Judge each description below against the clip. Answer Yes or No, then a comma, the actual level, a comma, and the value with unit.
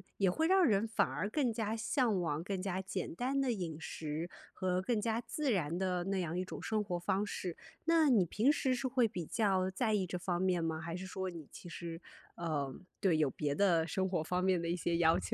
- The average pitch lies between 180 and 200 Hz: Yes, medium, 185 Hz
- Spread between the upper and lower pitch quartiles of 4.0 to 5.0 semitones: Yes, average, 4.3 semitones